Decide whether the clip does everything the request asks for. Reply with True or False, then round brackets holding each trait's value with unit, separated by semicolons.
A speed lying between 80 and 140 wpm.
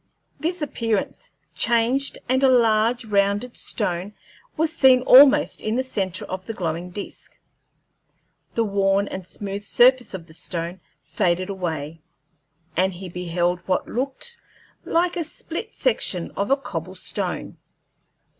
True (135 wpm)